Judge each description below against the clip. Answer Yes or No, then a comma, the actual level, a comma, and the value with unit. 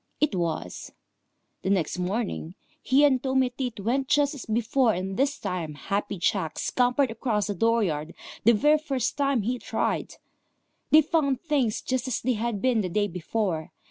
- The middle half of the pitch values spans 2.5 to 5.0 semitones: No, wide, 5.4 semitones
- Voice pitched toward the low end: No, high, 230 Hz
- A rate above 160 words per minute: Yes, average, 170 wpm